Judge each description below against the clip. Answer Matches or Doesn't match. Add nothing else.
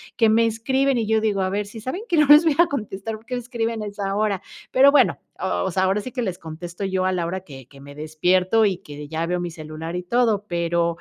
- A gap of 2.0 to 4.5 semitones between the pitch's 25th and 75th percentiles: Doesn't match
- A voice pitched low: Doesn't match